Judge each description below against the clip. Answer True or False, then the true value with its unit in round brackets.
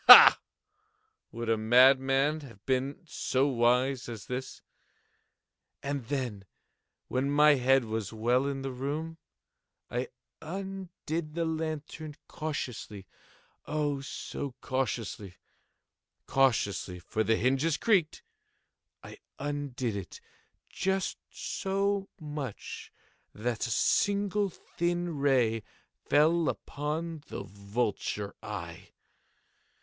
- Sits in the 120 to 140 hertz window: True (135 Hz)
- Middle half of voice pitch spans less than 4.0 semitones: False (4.9 semitones)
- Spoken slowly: True (90 wpm)